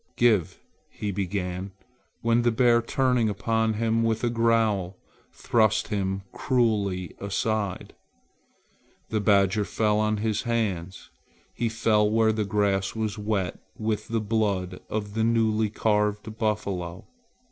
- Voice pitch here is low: Yes, low, 105 Hz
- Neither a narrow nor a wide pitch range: No, narrow, 2.1 semitones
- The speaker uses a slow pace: Yes, slow, 130 wpm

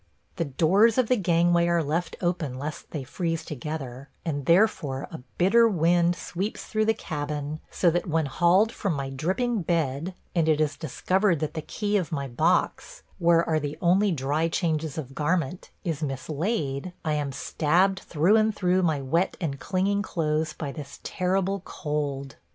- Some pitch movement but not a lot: Yes, average, 3.9 semitones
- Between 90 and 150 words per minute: No, average, 170 wpm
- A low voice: No, medium, 165 Hz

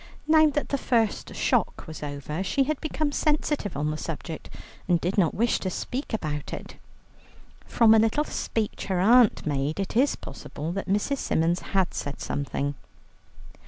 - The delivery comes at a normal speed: Yes, average, 165 wpm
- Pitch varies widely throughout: Yes, wide, 8.1 semitones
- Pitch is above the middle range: Yes, high, 195 Hz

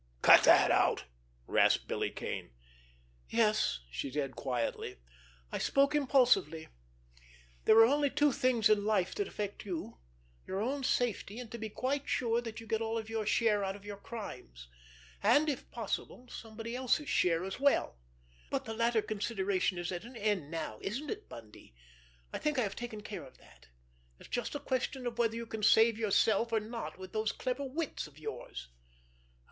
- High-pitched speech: Yes, high, 220 Hz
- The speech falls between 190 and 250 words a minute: No, average, 175 wpm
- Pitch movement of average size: Yes, average, 4.4 semitones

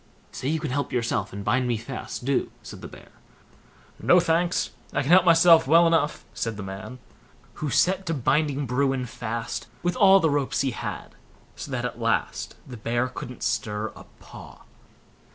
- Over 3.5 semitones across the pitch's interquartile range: Yes, wide, 5.5 semitones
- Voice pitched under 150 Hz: Yes, low, 135 Hz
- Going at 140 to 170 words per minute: No, average, 180 wpm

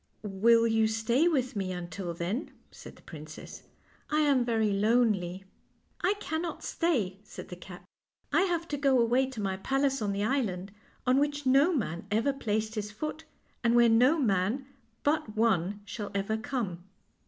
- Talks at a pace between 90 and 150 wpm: No, average, 180 wpm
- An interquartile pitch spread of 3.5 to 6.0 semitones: Yes, wide, 5.4 semitones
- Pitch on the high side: Yes, high, 225 Hz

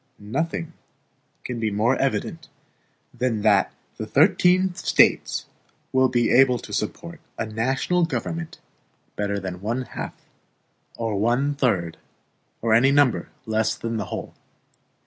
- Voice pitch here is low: Yes, low, 120 Hz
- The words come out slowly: Yes, slow, 125 wpm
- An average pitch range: Yes, average, 4.6 semitones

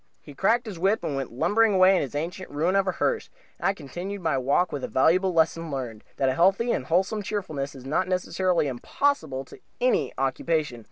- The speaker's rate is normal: No, fast, 210 wpm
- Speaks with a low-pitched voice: No, medium, 170 Hz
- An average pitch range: No, wide, 5.8 semitones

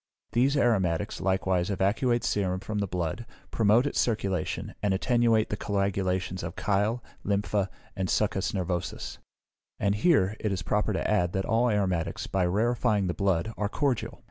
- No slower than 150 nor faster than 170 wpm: Yes, average, 155 wpm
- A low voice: Yes, low, 100 Hz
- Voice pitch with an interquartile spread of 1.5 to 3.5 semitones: Yes, average, 2.9 semitones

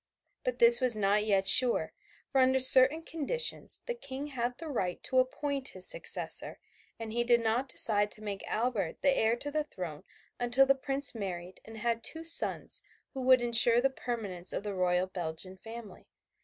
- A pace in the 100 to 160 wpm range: No, average, 185 wpm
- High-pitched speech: Yes, high, 240 Hz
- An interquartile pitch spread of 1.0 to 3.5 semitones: No, average, 4.7 semitones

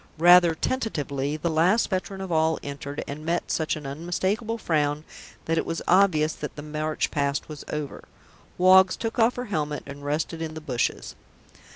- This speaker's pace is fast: No, average, 175 wpm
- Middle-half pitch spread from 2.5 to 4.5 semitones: Yes, average, 3.8 semitones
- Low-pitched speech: No, medium, 160 Hz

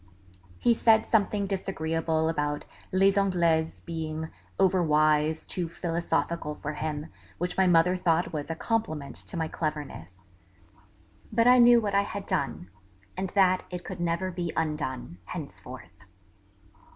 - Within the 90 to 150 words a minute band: Yes, average, 140 wpm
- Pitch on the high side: No, medium, 170 Hz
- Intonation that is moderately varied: Yes, average, 3.7 semitones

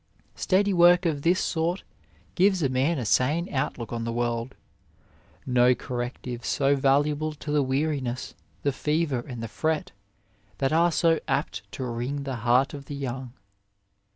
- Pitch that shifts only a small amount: No, average, 4.2 semitones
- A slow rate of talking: No, average, 155 wpm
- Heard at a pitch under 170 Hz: Yes, medium, 140 Hz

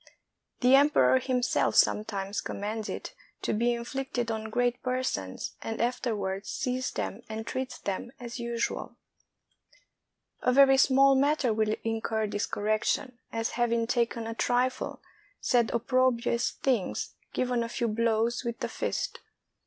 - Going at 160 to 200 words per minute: No, slow, 135 wpm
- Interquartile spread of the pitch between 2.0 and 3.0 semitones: Yes, narrow, 2.4 semitones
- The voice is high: Yes, high, 235 Hz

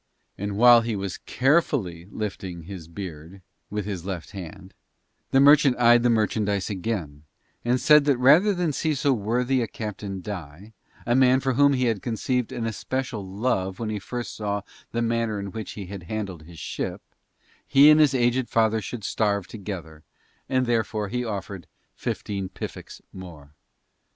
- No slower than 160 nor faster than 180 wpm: Yes, average, 165 wpm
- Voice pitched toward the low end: Yes, low, 110 Hz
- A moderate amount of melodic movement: Yes, average, 4.4 semitones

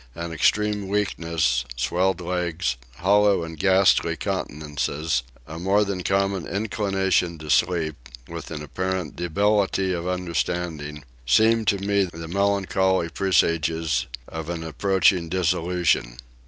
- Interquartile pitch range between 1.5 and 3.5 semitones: Yes, average, 3.1 semitones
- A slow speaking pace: Yes, slow, 115 wpm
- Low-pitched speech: Yes, very low, 90 Hz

